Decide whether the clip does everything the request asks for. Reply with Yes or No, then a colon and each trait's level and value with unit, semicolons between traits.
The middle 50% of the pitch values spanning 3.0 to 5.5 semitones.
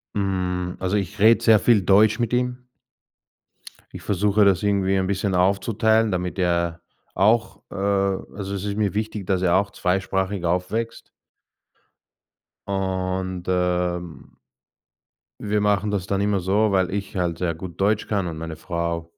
No: narrow, 2.4 semitones